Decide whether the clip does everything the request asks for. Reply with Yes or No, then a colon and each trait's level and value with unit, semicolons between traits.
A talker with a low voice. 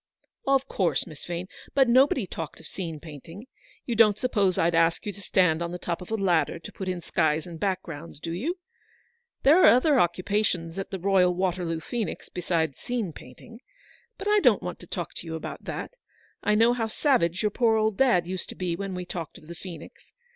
No: medium, 185 Hz